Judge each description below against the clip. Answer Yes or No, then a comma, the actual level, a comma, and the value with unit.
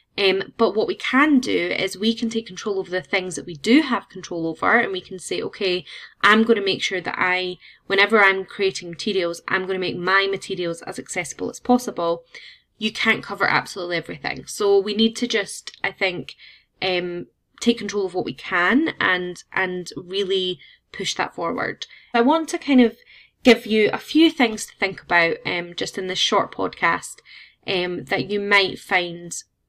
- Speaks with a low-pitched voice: No, high, 195 Hz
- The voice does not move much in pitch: No, average, 3.7 semitones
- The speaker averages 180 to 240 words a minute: Yes, average, 190 wpm